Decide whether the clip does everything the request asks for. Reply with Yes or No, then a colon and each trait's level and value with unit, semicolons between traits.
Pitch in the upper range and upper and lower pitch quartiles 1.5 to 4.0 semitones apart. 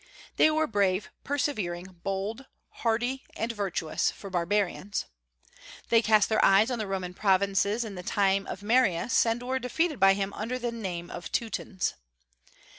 Yes: high, 205 Hz; average, 3.6 semitones